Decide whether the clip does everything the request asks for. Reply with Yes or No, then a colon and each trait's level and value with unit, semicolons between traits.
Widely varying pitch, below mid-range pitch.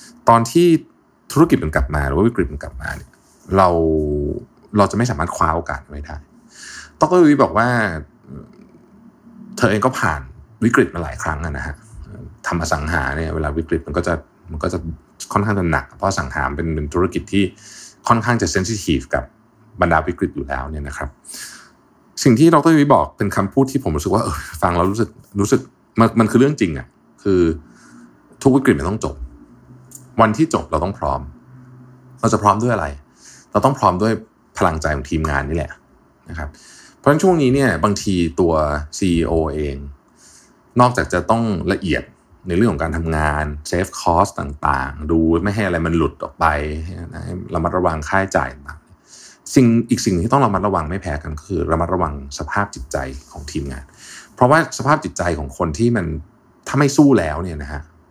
Yes: wide, 6.8 semitones; very low, 90 Hz